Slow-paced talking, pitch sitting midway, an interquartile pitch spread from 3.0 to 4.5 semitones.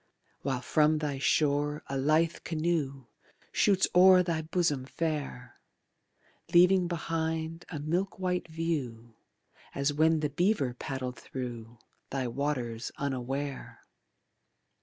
Yes: slow, 110 wpm; medium, 150 Hz; average, 3.8 semitones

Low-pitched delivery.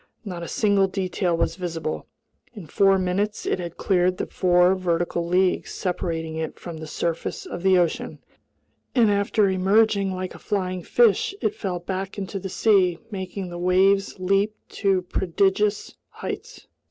No: medium, 185 Hz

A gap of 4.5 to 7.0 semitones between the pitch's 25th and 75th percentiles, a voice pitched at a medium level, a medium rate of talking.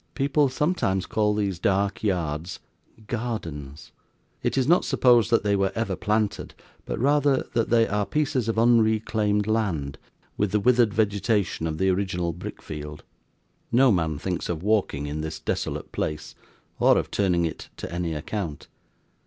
No: average, 5.1 semitones; low, 100 Hz; average, 155 wpm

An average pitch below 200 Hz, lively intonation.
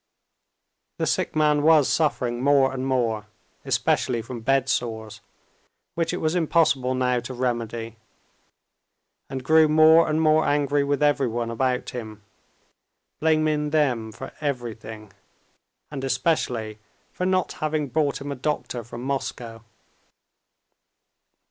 No: low, 135 Hz; average, 4.3 semitones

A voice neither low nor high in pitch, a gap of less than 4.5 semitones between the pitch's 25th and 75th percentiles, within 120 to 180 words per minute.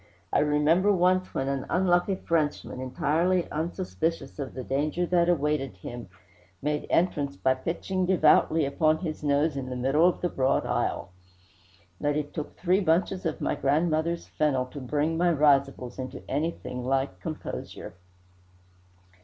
Yes: medium, 150 Hz; average, 3.9 semitones; average, 145 wpm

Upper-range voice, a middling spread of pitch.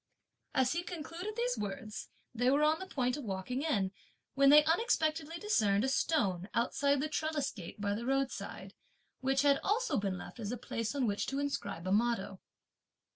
No: very high, 270 Hz; wide, 6.6 semitones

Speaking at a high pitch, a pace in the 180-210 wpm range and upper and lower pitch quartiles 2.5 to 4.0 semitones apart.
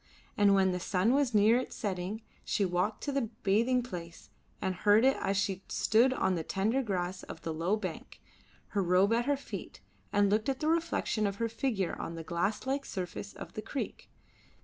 No: high, 205 Hz; average, 200 wpm; average, 4.5 semitones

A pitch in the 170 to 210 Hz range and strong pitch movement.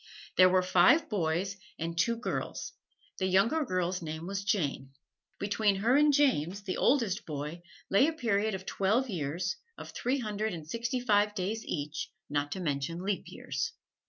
No: high, 190 Hz; average, 4.7 semitones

